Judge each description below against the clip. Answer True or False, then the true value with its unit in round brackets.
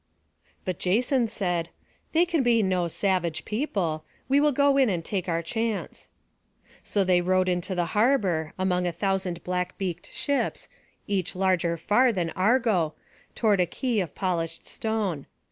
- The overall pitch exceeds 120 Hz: True (185 Hz)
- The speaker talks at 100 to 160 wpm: True (155 wpm)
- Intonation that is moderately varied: True (4.2 semitones)